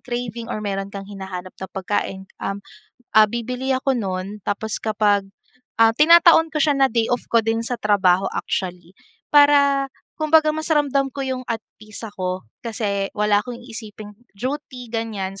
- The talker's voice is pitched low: No, high, 225 Hz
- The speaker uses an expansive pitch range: No, average, 4.7 semitones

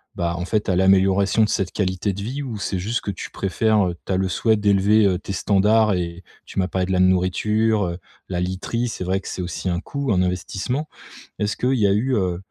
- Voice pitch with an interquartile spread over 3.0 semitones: No, average, 2.7 semitones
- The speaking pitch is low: Yes, very low, 95 Hz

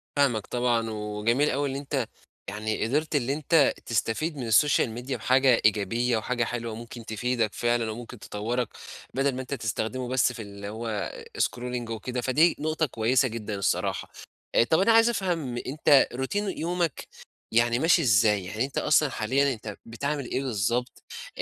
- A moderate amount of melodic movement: Yes, average, 3.9 semitones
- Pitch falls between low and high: No, low, 125 Hz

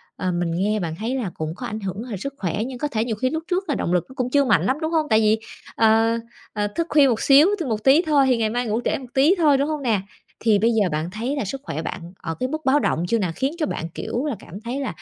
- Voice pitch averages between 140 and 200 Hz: No, high, 230 Hz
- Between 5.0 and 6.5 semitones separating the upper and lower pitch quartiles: Yes, average, 5.3 semitones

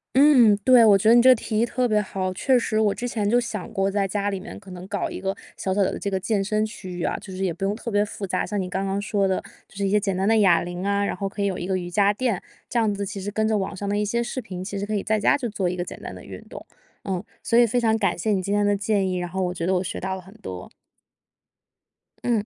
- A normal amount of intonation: No, narrow, 2.3 semitones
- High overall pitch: Yes, high, 200 Hz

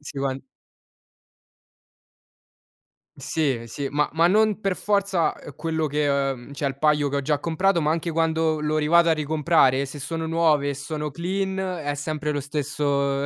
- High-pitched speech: No, medium, 150 Hz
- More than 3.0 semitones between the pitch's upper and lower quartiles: No, average, 2.7 semitones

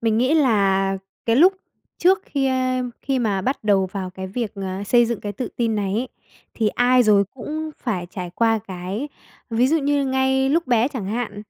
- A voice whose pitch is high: Yes, high, 230 Hz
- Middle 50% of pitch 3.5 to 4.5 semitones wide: No, average, 4.9 semitones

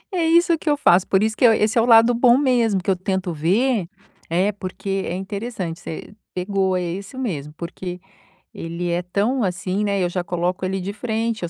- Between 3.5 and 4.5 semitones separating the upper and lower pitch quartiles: Yes, average, 4.1 semitones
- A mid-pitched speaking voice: No, high, 195 Hz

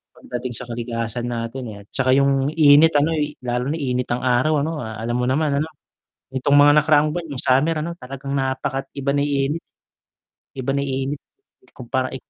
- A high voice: No, low, 135 Hz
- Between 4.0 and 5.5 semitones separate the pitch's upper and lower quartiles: No, average, 2.7 semitones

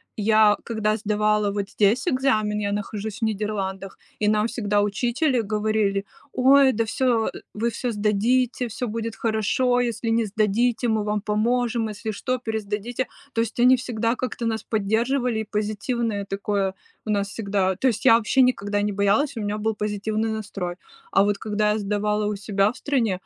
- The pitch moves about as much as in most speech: No, narrow, 2.3 semitones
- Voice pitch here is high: Yes, high, 215 Hz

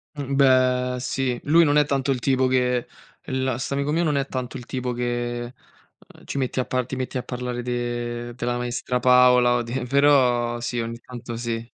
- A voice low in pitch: Yes, low, 125 Hz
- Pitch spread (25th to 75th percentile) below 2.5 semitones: Yes, narrow, 1.5 semitones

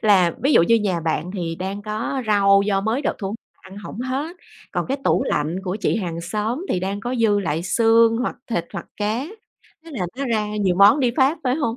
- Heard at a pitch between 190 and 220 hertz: Yes, high, 210 Hz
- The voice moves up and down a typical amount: Yes, average, 4.2 semitones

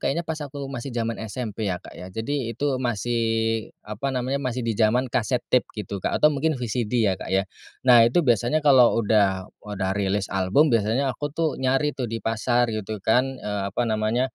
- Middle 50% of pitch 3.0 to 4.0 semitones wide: Yes, average, 3.5 semitones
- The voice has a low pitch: Yes, low, 120 Hz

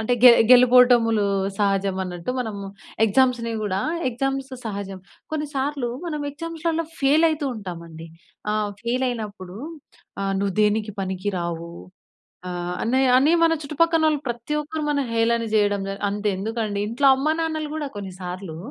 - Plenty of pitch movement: Yes, wide, 6.0 semitones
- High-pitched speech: Yes, high, 230 Hz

